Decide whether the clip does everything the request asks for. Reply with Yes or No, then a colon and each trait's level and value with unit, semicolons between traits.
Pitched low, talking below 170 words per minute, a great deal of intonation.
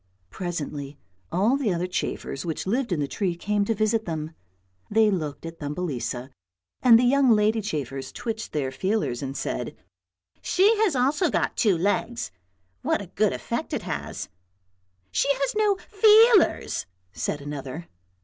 No: medium, 185 Hz; average, 160 wpm; wide, 8.9 semitones